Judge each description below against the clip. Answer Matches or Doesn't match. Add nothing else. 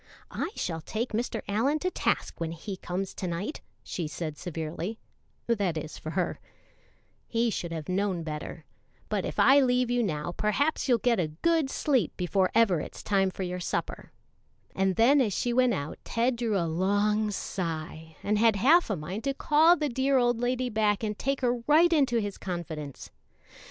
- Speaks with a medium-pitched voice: Doesn't match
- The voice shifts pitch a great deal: Matches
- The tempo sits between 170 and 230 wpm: Matches